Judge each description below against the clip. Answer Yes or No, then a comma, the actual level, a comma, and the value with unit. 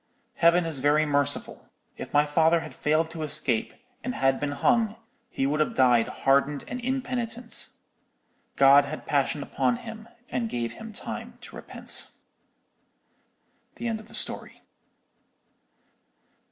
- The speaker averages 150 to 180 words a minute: No, average, 140 wpm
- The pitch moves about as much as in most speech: No, wide, 7.9 semitones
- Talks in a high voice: No, medium, 155 Hz